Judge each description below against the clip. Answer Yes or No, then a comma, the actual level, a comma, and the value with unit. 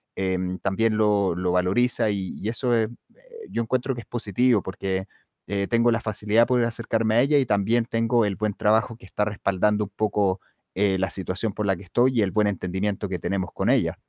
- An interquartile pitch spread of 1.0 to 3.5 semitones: Yes, average, 3.1 semitones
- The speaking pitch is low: Yes, low, 105 Hz